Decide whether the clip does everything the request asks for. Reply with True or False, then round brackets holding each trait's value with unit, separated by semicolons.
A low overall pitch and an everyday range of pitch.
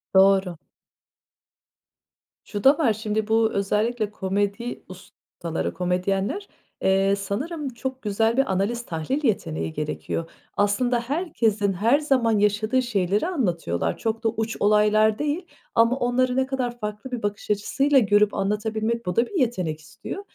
False (215 Hz; 3.7 semitones)